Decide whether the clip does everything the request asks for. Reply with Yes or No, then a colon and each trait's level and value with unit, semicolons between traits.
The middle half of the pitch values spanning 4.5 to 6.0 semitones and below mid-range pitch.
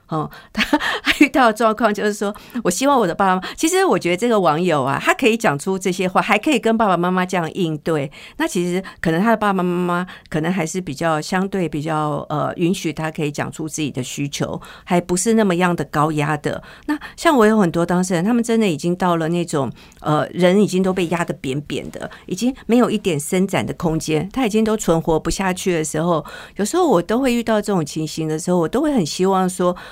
No: average, 5.1 semitones; medium, 180 Hz